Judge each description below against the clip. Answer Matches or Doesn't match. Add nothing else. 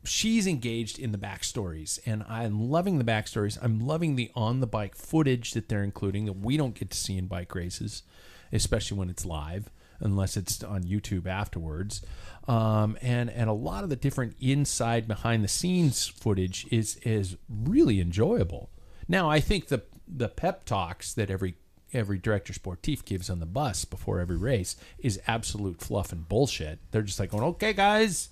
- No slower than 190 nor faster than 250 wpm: Doesn't match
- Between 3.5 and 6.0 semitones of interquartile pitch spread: Matches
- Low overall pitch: Matches